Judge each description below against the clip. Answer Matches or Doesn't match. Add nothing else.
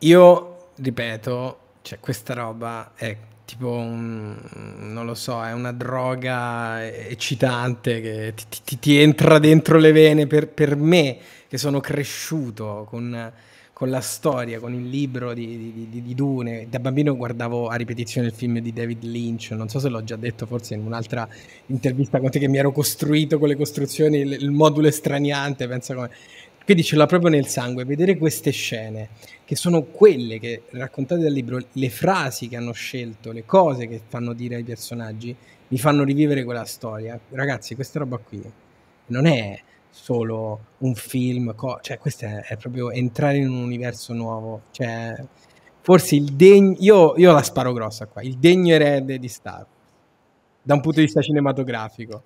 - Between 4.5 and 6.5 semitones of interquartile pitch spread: Doesn't match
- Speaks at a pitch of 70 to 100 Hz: Doesn't match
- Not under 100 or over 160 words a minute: Doesn't match